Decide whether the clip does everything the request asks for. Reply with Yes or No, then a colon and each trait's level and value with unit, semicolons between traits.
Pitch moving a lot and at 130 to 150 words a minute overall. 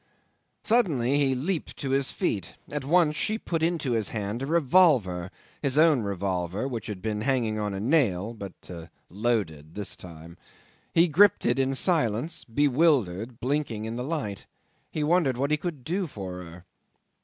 No: wide, 6.9 semitones; average, 165 wpm